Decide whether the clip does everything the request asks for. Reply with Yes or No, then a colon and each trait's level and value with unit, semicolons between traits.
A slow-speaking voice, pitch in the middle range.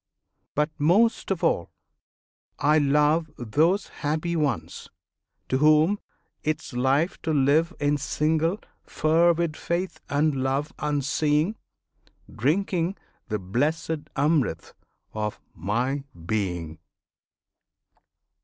Yes: slow, 95 wpm; medium, 150 Hz